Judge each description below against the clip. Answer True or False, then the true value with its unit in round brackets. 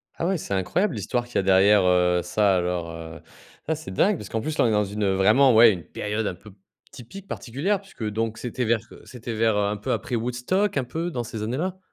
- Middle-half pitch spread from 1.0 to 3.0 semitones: False (4.9 semitones)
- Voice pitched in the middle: False (110 Hz)